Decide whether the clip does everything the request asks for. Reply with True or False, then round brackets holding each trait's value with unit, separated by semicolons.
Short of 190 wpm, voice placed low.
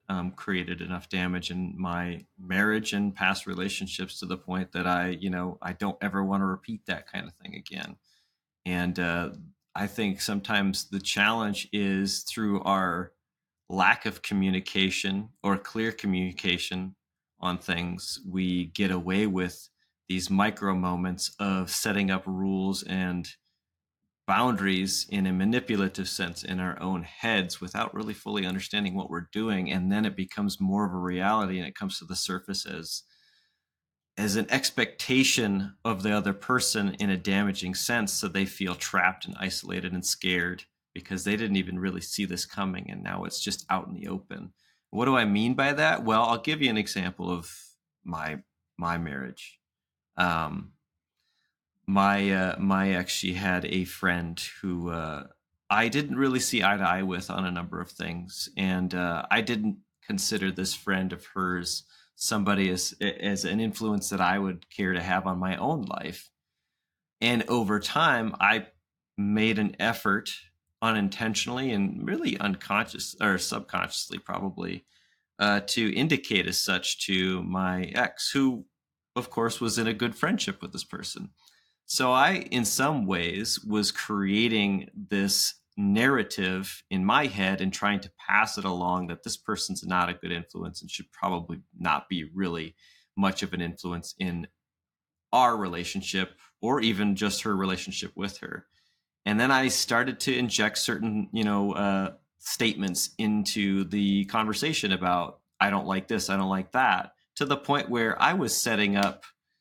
True (165 wpm; 95 Hz)